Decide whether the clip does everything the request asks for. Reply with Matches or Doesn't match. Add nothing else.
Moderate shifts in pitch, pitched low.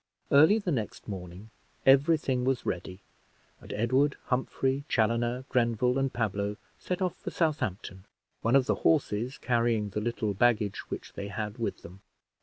Matches